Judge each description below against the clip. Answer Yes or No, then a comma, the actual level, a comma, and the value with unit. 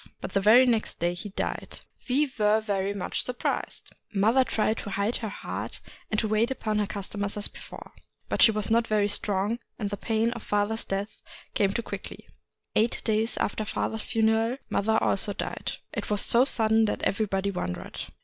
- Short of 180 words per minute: No, average, 185 wpm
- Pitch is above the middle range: Yes, high, 215 Hz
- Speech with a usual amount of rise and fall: No, narrow, 1.9 semitones